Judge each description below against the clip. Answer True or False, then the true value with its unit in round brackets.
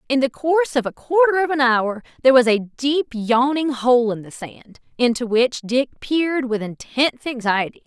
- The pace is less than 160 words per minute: False (190 wpm)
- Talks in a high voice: True (255 Hz)